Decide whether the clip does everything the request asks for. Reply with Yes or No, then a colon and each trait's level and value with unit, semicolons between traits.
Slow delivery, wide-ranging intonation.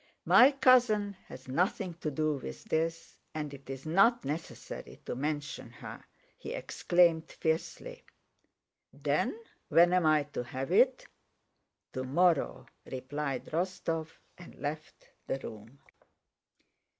No: slow, 115 wpm; average, 4.5 semitones